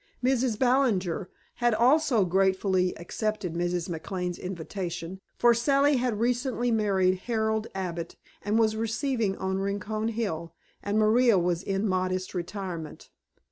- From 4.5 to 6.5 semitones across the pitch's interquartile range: No, average, 4.1 semitones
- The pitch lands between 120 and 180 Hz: No, high, 200 Hz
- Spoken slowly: Yes, slow, 125 wpm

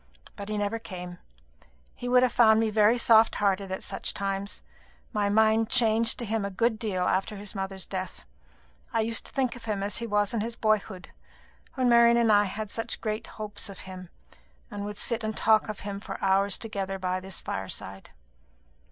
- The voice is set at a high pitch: Yes, high, 210 Hz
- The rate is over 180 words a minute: Yes, average, 195 wpm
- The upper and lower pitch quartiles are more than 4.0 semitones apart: No, narrow, 2.5 semitones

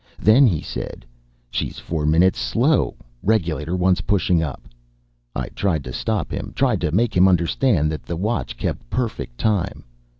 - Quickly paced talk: No, average, 165 wpm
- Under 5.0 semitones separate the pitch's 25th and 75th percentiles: No, wide, 5.5 semitones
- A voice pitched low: Yes, very low, 90 Hz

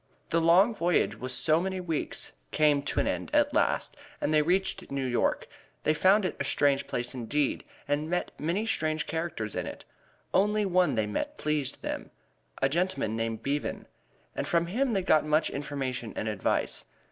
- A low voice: No, medium, 155 Hz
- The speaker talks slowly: No, average, 180 wpm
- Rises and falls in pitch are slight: No, average, 4.8 semitones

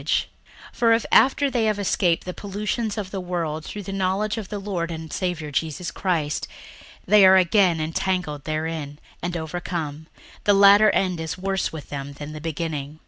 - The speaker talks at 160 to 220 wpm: Yes, average, 180 wpm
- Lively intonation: No, average, 3.9 semitones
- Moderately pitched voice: Yes, medium, 180 Hz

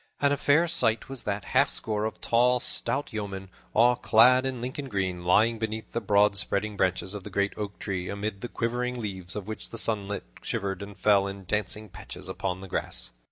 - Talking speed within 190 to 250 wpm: Yes, average, 200 wpm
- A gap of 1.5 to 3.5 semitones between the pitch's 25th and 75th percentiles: Yes, average, 3.1 semitones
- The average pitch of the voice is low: Yes, low, 105 Hz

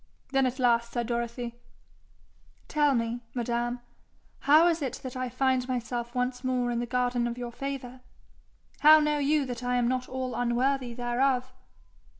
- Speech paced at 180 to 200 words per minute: No, average, 160 wpm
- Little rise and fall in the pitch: Yes, narrow, 1.6 semitones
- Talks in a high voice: Yes, very high, 250 Hz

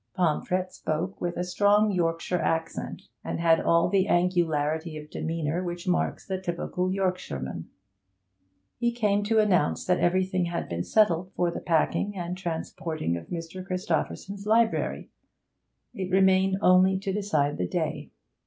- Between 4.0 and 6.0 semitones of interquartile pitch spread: No, narrow, 2.4 semitones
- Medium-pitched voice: Yes, medium, 180 Hz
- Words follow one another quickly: No, average, 145 wpm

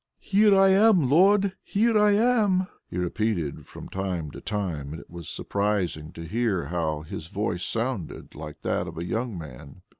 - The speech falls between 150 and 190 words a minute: Yes, average, 175 wpm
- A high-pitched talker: No, low, 100 Hz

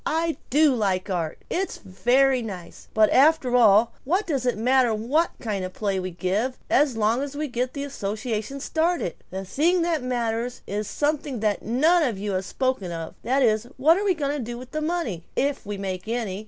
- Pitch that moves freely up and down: Yes, wide, 5.7 semitones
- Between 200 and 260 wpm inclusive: Yes, fast, 205 wpm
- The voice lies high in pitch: Yes, high, 245 Hz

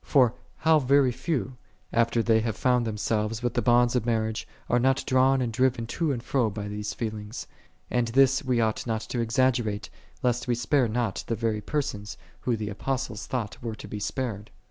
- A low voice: Yes, low, 120 Hz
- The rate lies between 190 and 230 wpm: Yes, average, 200 wpm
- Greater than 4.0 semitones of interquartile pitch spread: No, average, 2.8 semitones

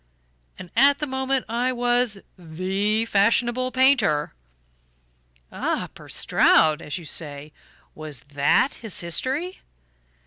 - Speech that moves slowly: Yes, slow, 110 wpm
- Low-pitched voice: No, high, 220 Hz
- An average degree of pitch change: No, wide, 8.2 semitones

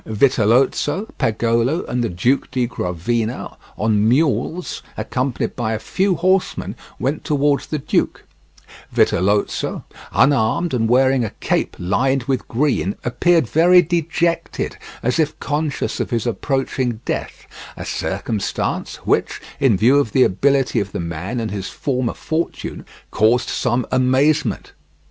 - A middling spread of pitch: Yes, average, 4.6 semitones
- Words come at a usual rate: No, slow, 130 wpm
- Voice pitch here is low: Yes, low, 130 Hz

